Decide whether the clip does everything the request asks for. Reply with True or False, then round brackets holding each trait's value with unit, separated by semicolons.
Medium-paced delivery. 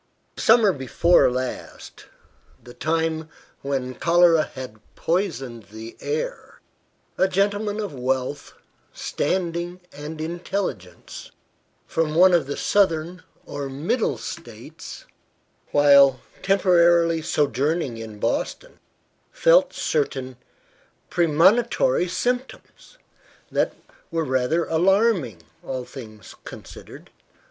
False (90 wpm)